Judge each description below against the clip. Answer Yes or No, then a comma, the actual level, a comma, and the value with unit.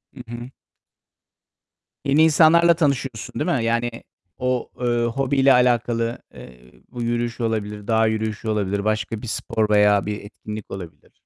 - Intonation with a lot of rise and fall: No, average, 2.8 semitones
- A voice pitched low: Yes, low, 115 Hz